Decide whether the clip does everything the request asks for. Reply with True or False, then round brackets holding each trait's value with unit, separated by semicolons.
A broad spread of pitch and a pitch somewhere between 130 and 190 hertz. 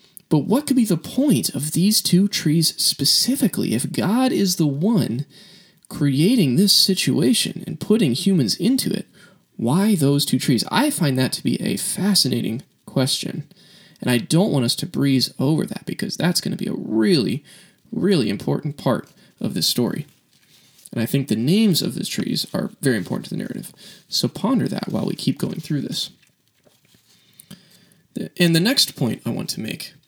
True (5.9 semitones; 185 Hz)